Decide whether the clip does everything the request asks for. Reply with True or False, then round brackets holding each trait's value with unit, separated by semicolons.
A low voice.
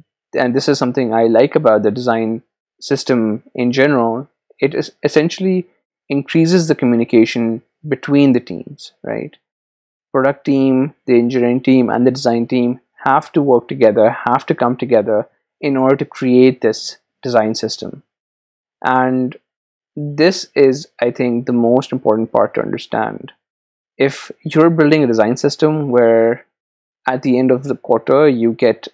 True (130 Hz)